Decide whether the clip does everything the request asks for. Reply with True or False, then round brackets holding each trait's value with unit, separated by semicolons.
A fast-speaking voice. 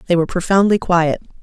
False (170 wpm)